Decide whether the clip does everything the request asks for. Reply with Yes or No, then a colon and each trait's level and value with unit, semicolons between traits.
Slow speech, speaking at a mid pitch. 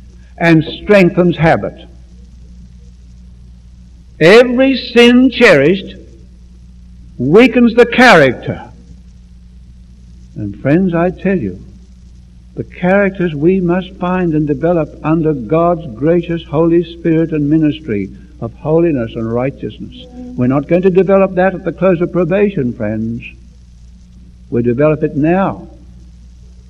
Yes: slow, 110 wpm; medium, 145 Hz